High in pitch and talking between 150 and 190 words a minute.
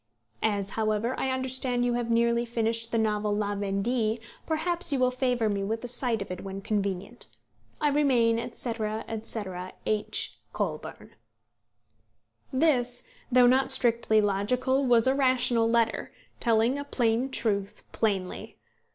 No: high, 235 Hz; average, 140 wpm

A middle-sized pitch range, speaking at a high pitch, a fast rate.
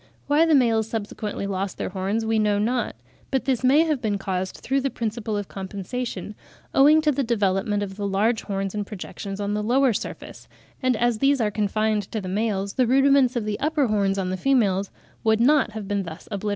Yes: average, 4.0 semitones; high, 215 Hz; fast, 210 wpm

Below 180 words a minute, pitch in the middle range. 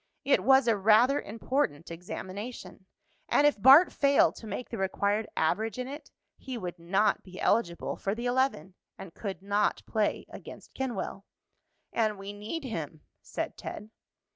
No: average, 155 wpm; high, 215 Hz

